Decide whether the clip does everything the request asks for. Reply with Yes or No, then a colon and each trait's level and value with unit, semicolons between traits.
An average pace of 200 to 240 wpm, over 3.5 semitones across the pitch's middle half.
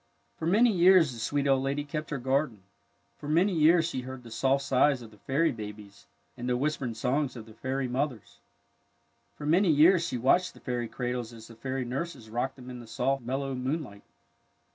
Yes: fast, 205 wpm; average, 3.9 semitones